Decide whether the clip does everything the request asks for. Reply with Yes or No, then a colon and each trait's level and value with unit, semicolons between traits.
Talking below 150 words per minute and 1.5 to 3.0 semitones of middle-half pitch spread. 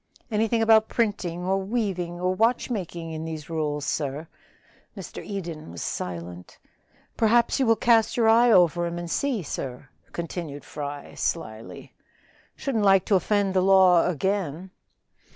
No: average, 140 wpm; average, 5.3 semitones